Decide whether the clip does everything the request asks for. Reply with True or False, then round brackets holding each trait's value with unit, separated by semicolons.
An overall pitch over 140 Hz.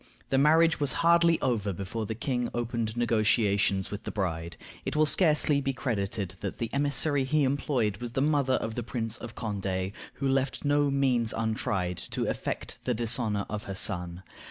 False (115 Hz)